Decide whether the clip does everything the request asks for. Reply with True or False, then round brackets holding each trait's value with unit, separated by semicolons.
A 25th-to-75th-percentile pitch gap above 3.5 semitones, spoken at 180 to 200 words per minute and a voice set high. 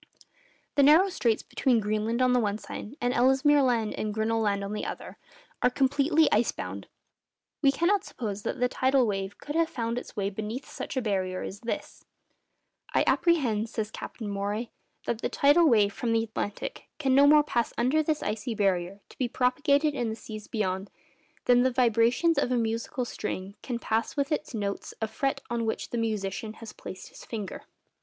True (4.2 semitones; 190 wpm; 230 Hz)